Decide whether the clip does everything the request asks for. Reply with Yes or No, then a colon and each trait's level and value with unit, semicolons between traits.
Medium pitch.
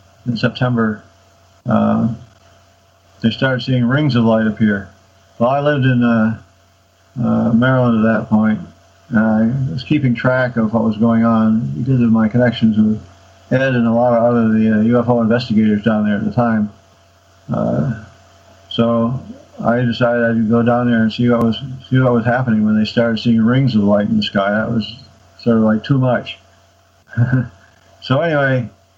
No: low, 115 Hz